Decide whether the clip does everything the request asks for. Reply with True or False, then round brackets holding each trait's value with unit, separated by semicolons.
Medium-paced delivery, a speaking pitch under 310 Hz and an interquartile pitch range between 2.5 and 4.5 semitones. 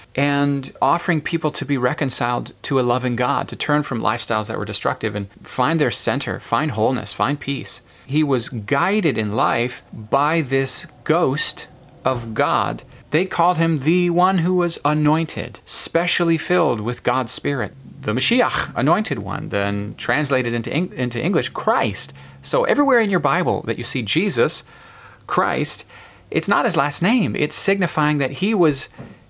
False (160 wpm; 140 Hz; 5.5 semitones)